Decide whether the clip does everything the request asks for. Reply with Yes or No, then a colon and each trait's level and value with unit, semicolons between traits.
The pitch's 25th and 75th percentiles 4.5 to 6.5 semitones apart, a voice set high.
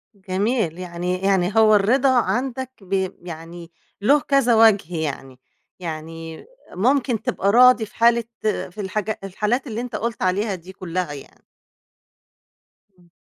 Yes: average, 4.9 semitones; high, 195 Hz